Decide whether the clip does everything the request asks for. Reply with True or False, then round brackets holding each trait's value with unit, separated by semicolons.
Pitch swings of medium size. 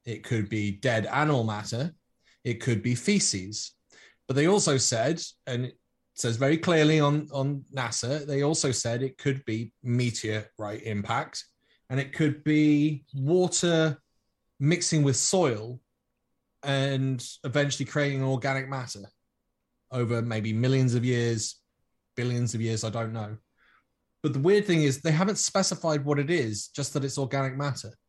True (4.2 semitones)